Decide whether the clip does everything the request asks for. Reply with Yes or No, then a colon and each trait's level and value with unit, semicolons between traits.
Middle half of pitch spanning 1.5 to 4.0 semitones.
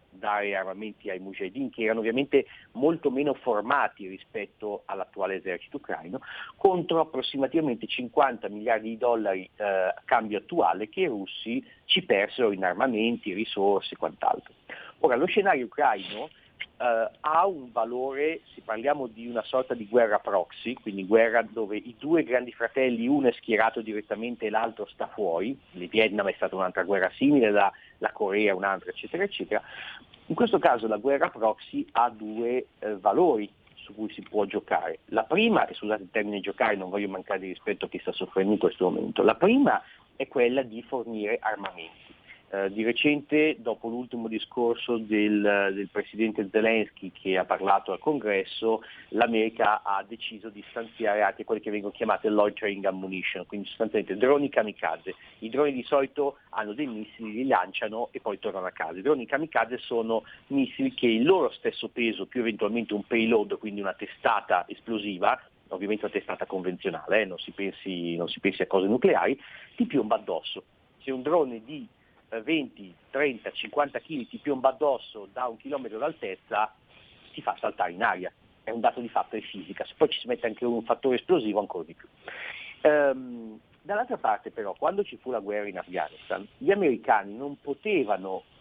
No: average, 4.4 semitones